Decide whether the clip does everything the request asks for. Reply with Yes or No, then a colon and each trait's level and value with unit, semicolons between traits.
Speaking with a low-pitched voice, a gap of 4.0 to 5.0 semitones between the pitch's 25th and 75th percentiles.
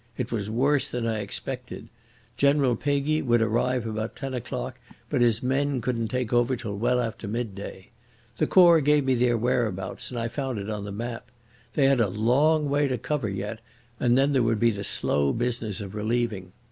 No: low, 120 Hz; average, 3.3 semitones